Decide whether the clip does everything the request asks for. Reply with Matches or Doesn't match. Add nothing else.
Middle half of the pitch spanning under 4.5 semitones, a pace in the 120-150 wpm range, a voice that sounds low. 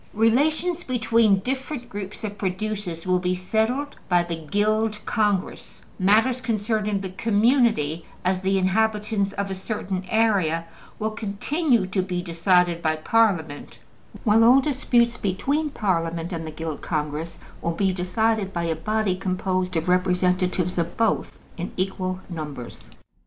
Doesn't match